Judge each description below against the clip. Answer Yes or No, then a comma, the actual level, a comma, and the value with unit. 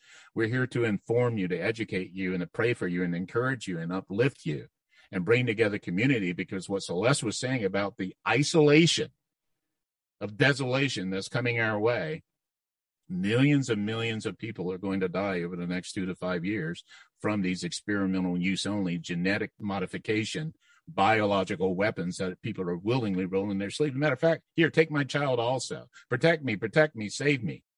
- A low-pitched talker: Yes, low, 110 Hz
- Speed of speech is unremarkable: Yes, average, 180 wpm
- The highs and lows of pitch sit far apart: Yes, wide, 8.3 semitones